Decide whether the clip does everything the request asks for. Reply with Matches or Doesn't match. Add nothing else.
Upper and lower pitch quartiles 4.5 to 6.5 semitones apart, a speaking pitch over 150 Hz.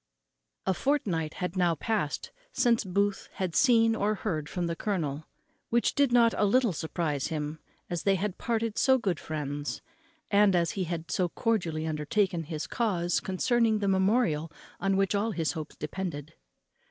Matches